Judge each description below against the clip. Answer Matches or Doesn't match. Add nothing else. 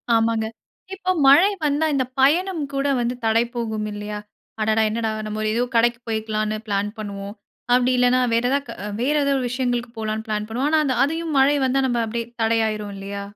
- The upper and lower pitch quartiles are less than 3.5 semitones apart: Doesn't match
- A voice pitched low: Doesn't match